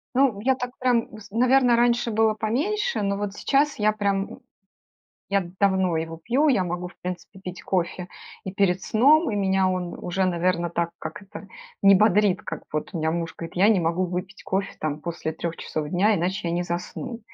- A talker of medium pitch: No, high, 195 Hz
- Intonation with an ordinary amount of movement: Yes, average, 4.1 semitones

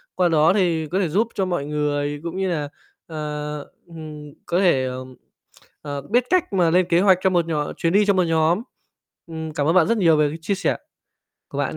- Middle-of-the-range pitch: Yes, medium, 165 Hz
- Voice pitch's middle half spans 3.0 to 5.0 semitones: Yes, average, 3.6 semitones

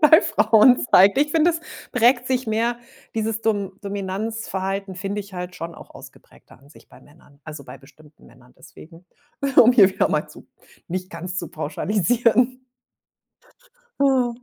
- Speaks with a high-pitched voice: Yes, high, 200 Hz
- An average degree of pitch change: No, wide, 5.9 semitones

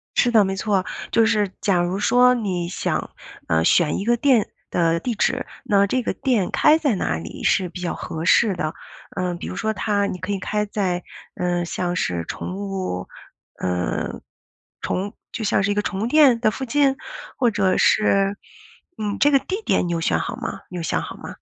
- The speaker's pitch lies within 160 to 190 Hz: No, high, 200 Hz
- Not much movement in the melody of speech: No, average, 4.2 semitones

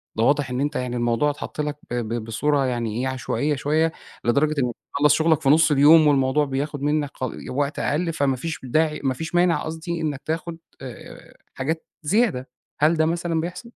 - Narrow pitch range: No, average, 3.3 semitones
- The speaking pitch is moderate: Yes, medium, 145 Hz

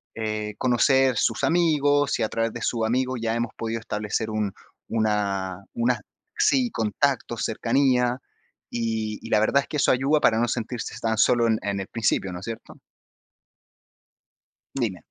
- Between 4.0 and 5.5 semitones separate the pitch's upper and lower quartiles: No, average, 2.9 semitones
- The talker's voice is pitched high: No, low, 115 Hz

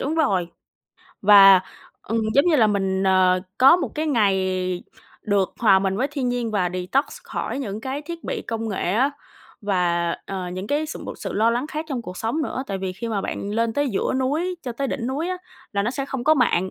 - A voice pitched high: Yes, high, 225 Hz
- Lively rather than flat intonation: Yes, wide, 6.2 semitones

